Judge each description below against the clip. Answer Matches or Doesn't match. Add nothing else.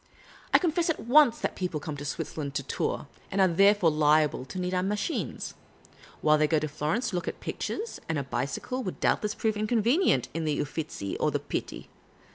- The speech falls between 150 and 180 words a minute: Doesn't match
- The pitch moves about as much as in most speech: Doesn't match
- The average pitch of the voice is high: Doesn't match